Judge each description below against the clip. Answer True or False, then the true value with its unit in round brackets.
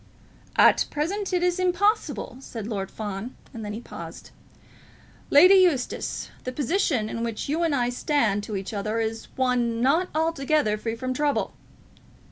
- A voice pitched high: True (255 Hz)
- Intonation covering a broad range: True (6.4 semitones)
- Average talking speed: True (155 wpm)